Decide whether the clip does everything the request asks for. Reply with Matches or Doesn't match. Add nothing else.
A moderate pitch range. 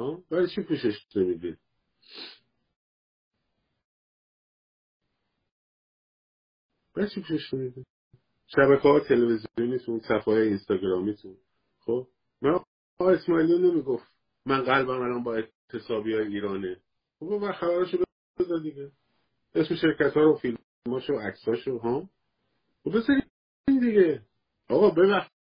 Doesn't match